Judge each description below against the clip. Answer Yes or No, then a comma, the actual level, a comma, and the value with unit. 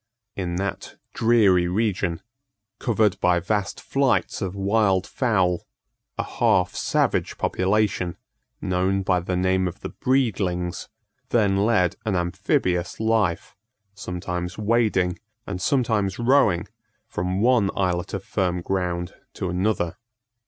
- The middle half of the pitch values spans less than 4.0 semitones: Yes, average, 3.2 semitones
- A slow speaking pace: Yes, slow, 115 wpm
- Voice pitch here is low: Yes, very low, 95 Hz